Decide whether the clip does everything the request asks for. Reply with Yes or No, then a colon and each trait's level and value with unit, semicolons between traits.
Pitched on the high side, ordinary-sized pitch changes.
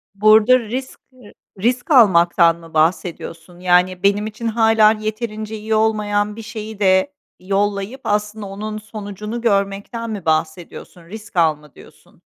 Yes: high, 210 Hz; average, 3.0 semitones